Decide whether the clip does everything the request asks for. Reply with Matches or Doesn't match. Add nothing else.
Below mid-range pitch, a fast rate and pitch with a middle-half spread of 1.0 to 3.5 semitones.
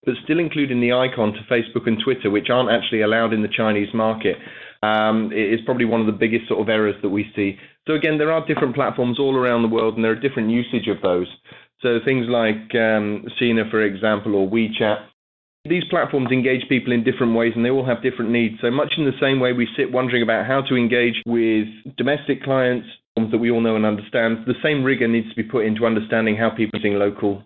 Matches